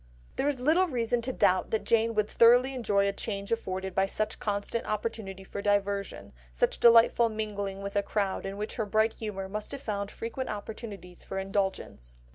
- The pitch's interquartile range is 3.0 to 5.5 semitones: No, narrow, 2.6 semitones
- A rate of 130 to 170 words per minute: No, average, 185 wpm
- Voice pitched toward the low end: No, high, 210 Hz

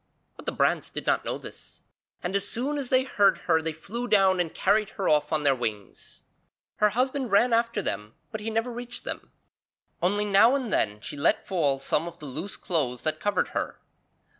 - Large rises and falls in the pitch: Yes, wide, 7.0 semitones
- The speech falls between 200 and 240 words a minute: Yes, fast, 205 wpm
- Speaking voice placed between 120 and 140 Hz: No, high, 195 Hz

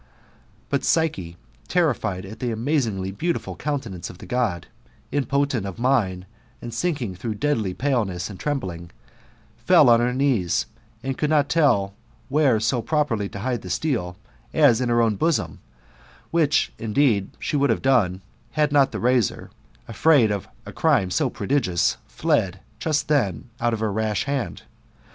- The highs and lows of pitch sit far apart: Yes, wide, 6.4 semitones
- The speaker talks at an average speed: Yes, average, 155 wpm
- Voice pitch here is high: No, low, 120 Hz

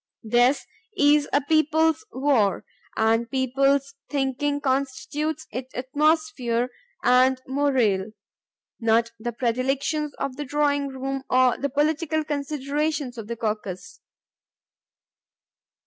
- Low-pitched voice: No, very high, 270 Hz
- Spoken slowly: Yes, slow, 105 wpm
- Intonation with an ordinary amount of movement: Yes, average, 3.1 semitones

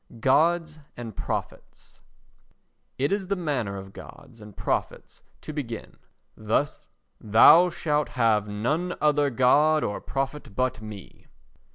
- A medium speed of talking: No, slow, 120 wpm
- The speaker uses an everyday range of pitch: No, wide, 5.8 semitones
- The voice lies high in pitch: No, low, 135 Hz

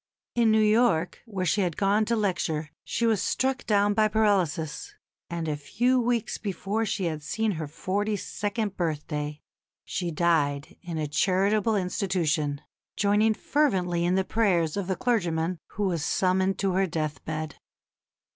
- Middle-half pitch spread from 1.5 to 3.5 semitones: No, average, 4.7 semitones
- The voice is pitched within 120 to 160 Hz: No, high, 190 Hz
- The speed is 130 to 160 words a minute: Yes, average, 155 wpm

